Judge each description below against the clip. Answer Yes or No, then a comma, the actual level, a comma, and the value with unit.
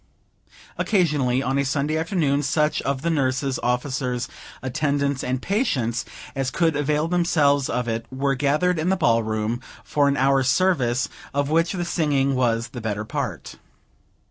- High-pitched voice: No, medium, 140 Hz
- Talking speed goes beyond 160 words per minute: No, average, 155 wpm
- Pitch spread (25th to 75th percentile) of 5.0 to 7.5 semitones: No, average, 3.5 semitones